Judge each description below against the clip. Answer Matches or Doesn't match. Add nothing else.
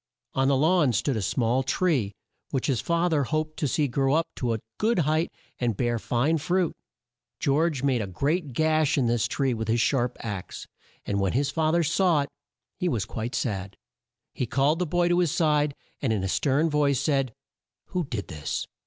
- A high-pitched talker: Doesn't match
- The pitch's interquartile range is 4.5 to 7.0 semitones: Matches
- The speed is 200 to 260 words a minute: Matches